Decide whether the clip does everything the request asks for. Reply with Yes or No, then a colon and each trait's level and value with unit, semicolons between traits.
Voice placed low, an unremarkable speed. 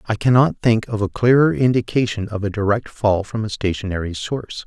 Yes: low, 110 Hz; average, 195 wpm